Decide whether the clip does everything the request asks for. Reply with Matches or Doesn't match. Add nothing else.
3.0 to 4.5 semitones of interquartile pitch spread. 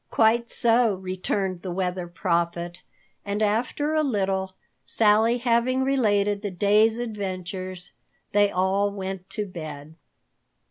Matches